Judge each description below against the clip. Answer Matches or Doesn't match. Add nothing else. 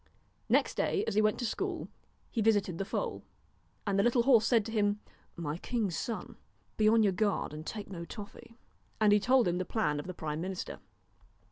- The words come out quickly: Matches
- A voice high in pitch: Matches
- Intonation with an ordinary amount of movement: Matches